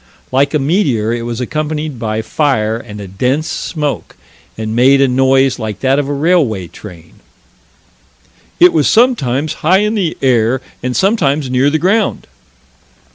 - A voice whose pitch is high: No, low, 135 Hz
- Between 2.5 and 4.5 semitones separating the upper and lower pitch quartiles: No, average, 5.0 semitones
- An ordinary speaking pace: Yes, average, 155 wpm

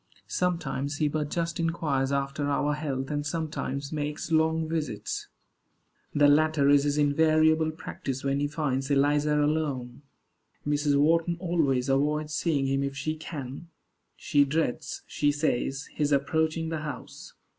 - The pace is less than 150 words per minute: Yes, average, 140 wpm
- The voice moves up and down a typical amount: No, narrow, 2.1 semitones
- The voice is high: No, medium, 145 Hz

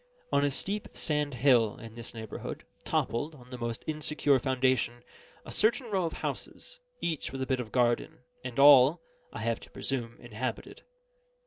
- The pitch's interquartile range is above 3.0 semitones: Yes, average, 3.9 semitones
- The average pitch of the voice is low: Yes, low, 130 Hz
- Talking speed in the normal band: Yes, average, 170 wpm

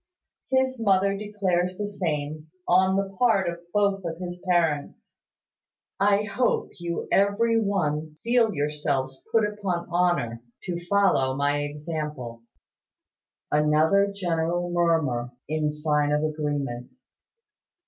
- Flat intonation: No, average, 4.9 semitones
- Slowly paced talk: Yes, slow, 115 wpm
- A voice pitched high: No, medium, 175 Hz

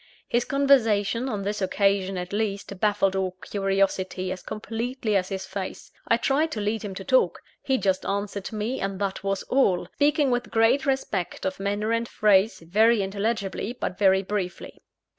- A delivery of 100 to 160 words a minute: No, average, 170 wpm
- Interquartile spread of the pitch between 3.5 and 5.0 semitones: No, average, 3.1 semitones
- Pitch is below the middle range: No, high, 205 Hz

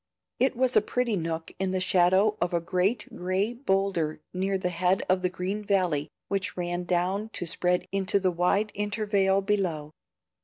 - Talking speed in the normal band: Yes, average, 170 wpm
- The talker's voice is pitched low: No, high, 190 Hz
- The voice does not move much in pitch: Yes, narrow, 2.1 semitones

